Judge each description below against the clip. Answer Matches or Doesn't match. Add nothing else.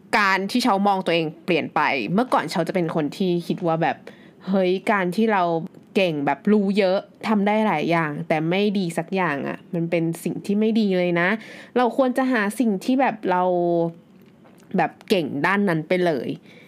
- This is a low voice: Doesn't match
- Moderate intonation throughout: Matches